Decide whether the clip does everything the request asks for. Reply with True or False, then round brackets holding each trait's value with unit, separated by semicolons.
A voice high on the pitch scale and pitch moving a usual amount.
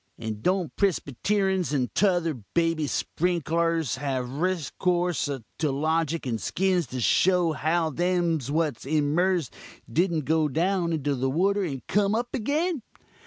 False (165 Hz; 4.1 semitones)